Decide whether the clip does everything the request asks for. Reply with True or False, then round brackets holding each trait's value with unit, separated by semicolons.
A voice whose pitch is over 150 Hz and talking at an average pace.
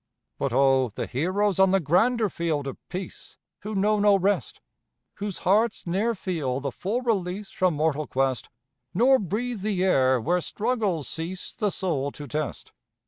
True (185 Hz; 160 wpm)